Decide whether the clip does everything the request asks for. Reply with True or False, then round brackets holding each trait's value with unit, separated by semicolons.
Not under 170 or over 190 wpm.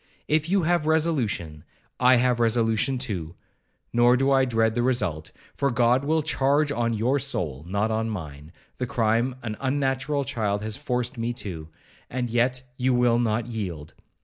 False (160 wpm)